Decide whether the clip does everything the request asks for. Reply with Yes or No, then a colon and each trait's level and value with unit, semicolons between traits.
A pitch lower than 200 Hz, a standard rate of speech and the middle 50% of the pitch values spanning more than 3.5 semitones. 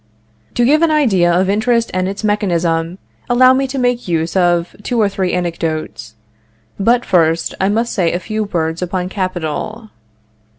Yes: high, 190 Hz; average, 165 wpm; average, 5.1 semitones